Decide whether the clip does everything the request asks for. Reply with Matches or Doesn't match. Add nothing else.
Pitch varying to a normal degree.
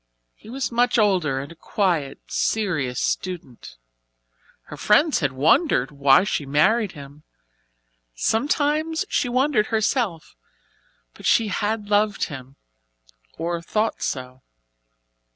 Doesn't match